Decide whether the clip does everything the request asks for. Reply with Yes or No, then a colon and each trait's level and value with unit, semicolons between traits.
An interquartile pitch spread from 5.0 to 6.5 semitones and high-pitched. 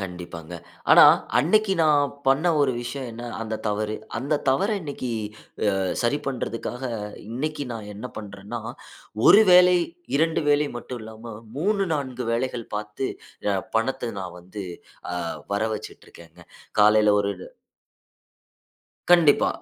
No: wide, 5.6 semitones; low, 125 Hz